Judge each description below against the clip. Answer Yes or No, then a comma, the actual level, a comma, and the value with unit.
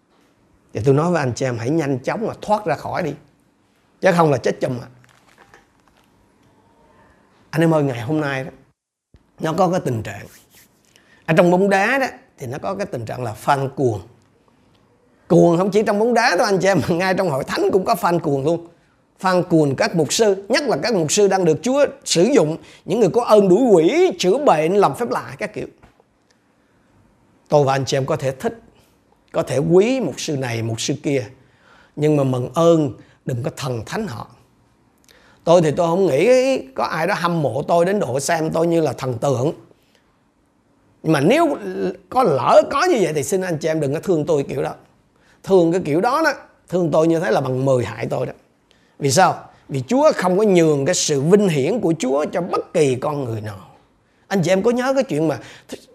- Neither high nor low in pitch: Yes, medium, 165 Hz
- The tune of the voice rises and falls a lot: Yes, wide, 5.9 semitones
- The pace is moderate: Yes, average, 215 wpm